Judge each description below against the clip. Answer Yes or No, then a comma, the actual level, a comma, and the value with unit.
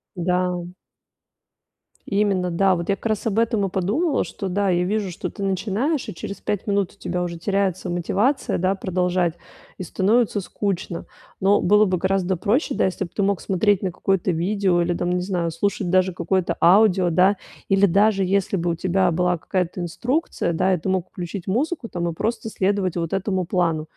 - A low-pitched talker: No, high, 190 Hz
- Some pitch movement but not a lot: No, narrow, 2.3 semitones